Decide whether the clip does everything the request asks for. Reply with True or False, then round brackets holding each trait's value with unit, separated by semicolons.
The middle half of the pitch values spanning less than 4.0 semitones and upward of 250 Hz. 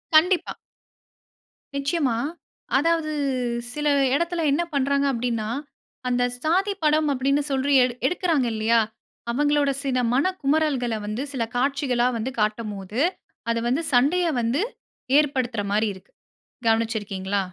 False (4.5 semitones; 270 Hz)